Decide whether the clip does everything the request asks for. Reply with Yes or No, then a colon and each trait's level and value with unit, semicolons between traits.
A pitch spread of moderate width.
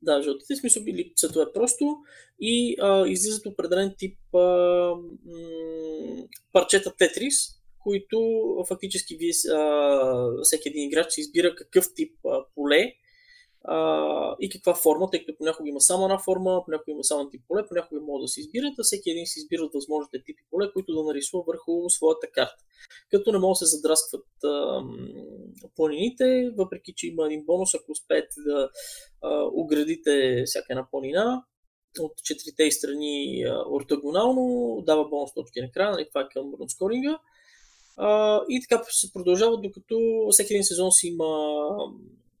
No: wide, 6.9 semitones